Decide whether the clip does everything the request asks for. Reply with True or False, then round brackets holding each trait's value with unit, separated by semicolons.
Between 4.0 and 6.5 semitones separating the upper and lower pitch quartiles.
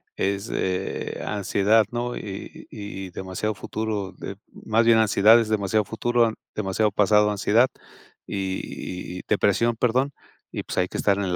False (2.5 semitones)